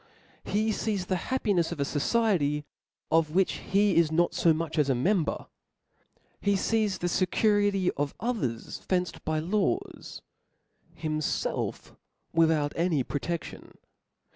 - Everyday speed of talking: No, slow, 120 wpm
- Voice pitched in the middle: Yes, medium, 175 Hz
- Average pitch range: Yes, average, 4.7 semitones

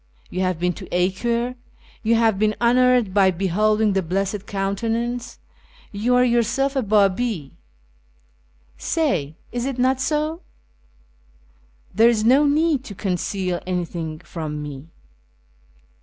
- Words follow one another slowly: Yes, slow, 125 wpm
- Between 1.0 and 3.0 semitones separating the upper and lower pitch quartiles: No, average, 5.0 semitones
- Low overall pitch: No, high, 215 Hz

